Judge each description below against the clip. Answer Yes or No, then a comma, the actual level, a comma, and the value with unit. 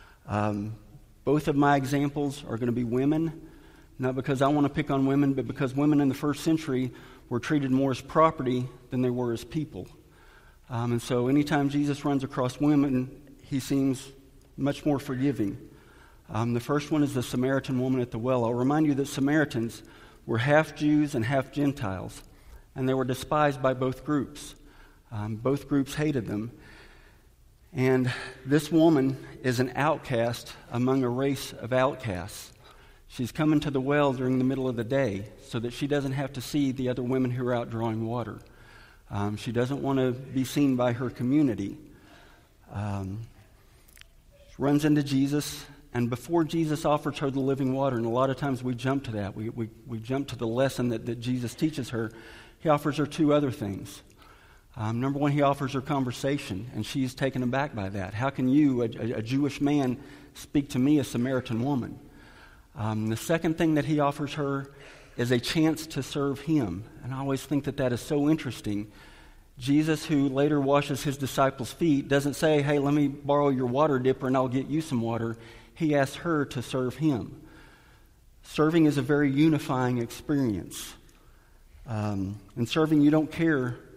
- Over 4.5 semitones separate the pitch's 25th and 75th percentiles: No, average, 3.1 semitones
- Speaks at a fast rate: No, average, 185 wpm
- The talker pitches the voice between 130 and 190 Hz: Yes, low, 135 Hz